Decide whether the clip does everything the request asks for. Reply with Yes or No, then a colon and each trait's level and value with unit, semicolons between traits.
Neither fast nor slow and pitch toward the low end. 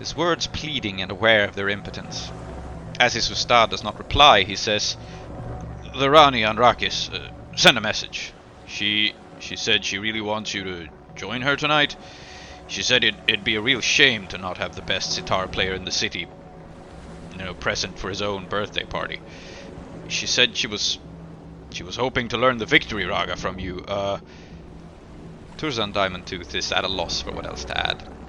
Yes: average, 185 wpm; low, 100 Hz